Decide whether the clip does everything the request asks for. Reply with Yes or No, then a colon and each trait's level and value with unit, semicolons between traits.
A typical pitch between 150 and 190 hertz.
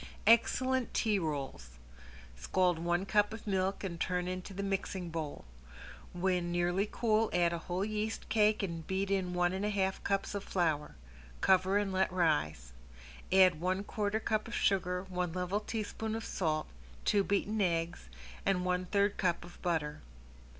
Yes: medium, 185 Hz